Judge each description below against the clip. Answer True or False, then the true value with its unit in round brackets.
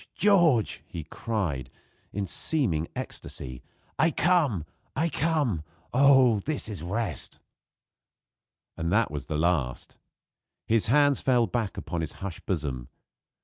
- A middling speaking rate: False (120 wpm)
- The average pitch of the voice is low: True (105 Hz)